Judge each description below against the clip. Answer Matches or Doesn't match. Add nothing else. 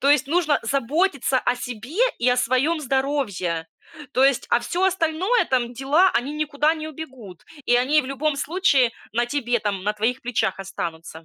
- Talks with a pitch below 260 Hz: Doesn't match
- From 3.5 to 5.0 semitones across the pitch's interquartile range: Matches